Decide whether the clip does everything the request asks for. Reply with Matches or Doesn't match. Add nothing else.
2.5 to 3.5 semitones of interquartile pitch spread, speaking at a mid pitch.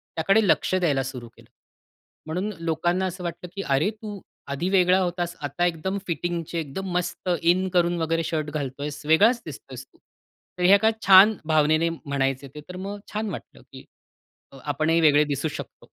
Doesn't match